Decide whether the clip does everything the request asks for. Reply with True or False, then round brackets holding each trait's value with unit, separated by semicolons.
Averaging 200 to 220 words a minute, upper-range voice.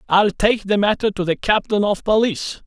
True (205 wpm; 205 Hz)